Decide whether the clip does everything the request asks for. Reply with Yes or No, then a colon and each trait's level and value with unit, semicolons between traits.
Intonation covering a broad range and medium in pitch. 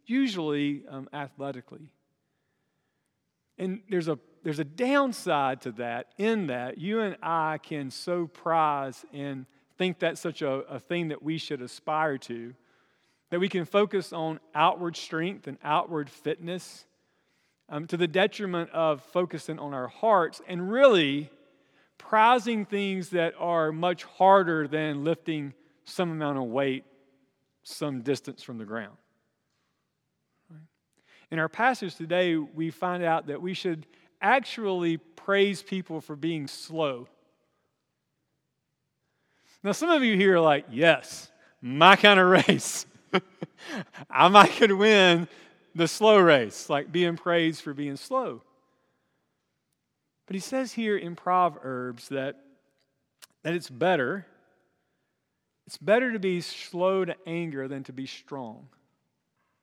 No: average, 4.4 semitones; medium, 165 Hz